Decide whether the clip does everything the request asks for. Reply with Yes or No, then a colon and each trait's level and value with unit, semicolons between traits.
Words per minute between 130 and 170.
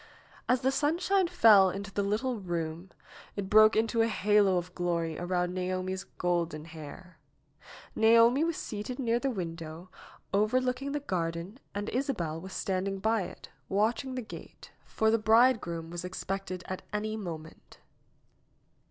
Yes: average, 145 wpm